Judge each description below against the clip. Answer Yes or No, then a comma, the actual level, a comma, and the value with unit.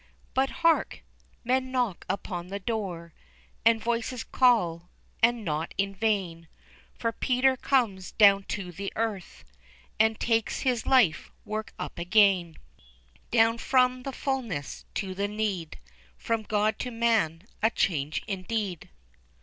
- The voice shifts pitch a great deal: No, average, 4.2 semitones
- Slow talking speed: Yes, slow, 130 wpm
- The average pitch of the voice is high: Yes, high, 215 Hz